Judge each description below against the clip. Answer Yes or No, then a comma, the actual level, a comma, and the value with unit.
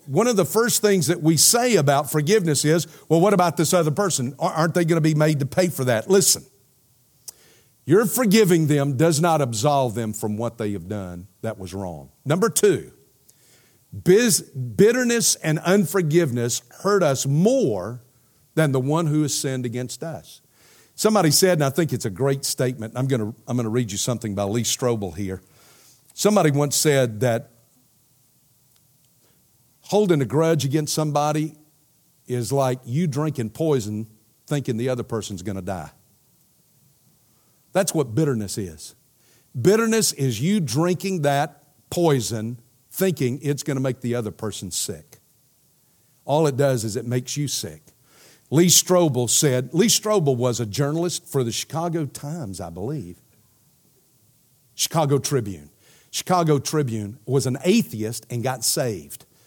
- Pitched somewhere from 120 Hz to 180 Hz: Yes, medium, 140 Hz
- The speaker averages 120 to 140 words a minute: No, average, 155 wpm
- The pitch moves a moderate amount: Yes, average, 5.0 semitones